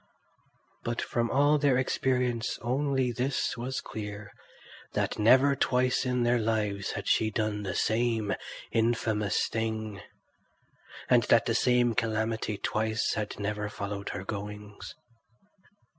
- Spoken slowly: Yes, slow, 125 wpm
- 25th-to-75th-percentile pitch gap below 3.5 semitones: Yes, average, 3.0 semitones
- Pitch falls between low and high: No, low, 110 Hz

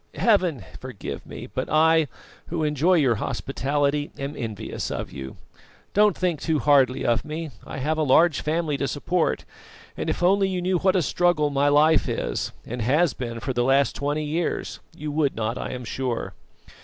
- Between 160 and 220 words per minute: Yes, average, 180 wpm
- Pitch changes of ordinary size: Yes, average, 3.7 semitones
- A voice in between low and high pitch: Yes, medium, 150 Hz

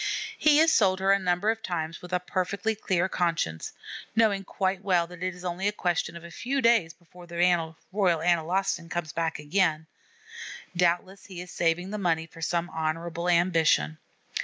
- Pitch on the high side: No, medium, 175 Hz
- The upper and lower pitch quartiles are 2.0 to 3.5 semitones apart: Yes, narrow, 2.4 semitones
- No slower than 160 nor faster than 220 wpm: Yes, average, 180 wpm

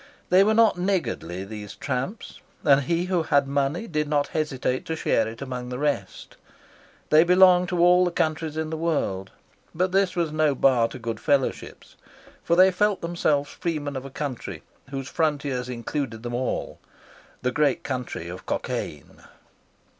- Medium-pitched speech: Yes, medium, 145 Hz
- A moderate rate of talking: Yes, average, 165 wpm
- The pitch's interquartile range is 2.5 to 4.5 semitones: No, average, 5.2 semitones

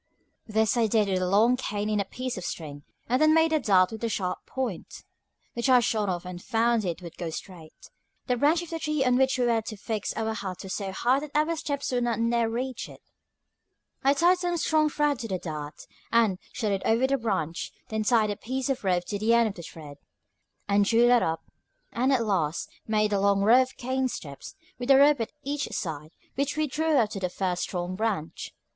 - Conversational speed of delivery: No, fast, 230 wpm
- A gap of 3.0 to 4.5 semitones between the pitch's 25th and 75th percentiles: No, average, 5.3 semitones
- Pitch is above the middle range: Yes, high, 225 Hz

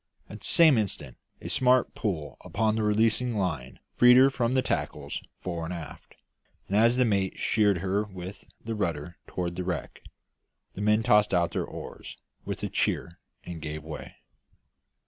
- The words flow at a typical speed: Yes, average, 170 wpm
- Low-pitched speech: Yes, low, 100 Hz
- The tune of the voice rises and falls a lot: No, average, 4.7 semitones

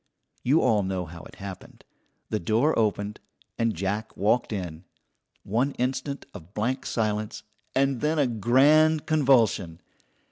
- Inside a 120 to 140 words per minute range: Yes, slow, 135 wpm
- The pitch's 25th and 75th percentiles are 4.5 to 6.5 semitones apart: Yes, average, 5.0 semitones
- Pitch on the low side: Yes, low, 110 Hz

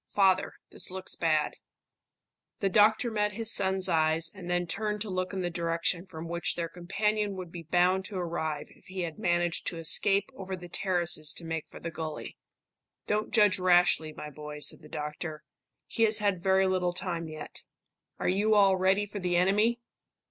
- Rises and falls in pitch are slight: No, average, 3.0 semitones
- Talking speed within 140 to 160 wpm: No, average, 185 wpm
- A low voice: No, medium, 180 Hz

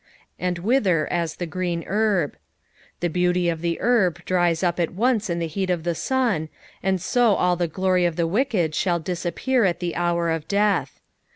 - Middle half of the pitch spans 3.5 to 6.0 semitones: No, narrow, 2.6 semitones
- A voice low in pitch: No, medium, 180 Hz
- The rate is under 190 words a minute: No, average, 200 wpm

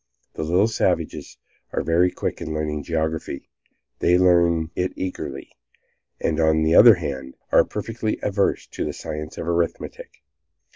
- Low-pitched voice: Yes, very low, 85 Hz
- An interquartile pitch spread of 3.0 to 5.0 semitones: No, narrow, 2.6 semitones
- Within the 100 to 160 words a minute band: Yes, average, 145 wpm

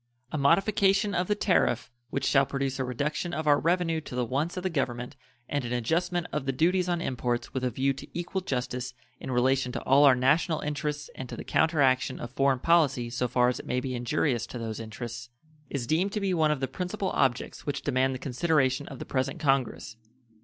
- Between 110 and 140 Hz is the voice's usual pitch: Yes, low, 135 Hz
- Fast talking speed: Yes, fast, 215 wpm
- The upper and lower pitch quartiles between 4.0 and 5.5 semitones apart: Yes, average, 4.4 semitones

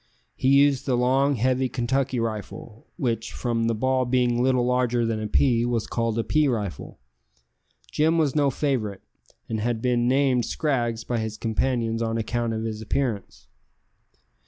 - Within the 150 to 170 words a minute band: Yes, average, 160 wpm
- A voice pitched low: Yes, low, 120 Hz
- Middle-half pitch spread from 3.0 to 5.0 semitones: No, narrow, 2.5 semitones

